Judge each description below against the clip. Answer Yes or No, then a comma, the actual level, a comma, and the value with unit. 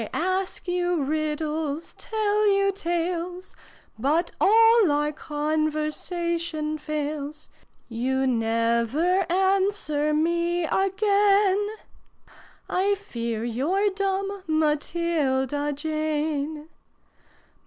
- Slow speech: Yes, slow, 80 wpm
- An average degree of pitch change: Yes, average, 4.4 semitones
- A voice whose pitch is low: No, very high, 320 Hz